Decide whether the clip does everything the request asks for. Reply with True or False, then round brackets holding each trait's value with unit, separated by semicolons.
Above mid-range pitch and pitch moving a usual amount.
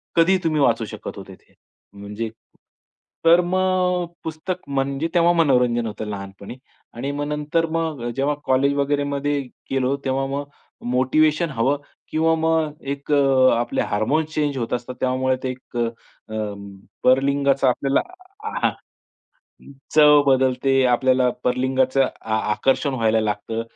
False (135 Hz; 3.2 semitones)